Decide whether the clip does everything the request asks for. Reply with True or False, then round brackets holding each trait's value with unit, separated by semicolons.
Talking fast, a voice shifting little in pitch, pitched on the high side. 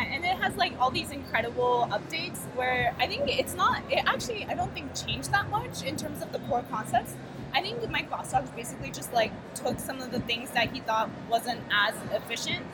True (215 wpm; 1.5 semitones; 245 Hz)